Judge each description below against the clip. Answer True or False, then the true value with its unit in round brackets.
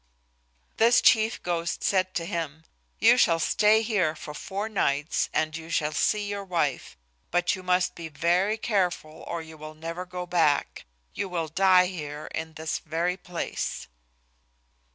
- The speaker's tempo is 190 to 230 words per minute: False (155 wpm)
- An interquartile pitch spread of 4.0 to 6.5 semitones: False (3.3 semitones)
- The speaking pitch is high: False (175 Hz)